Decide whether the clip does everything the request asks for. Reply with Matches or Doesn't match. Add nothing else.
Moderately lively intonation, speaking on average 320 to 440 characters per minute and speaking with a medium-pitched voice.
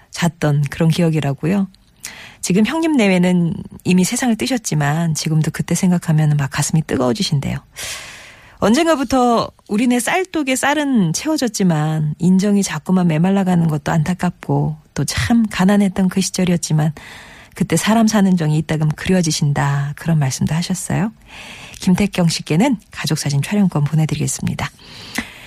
Matches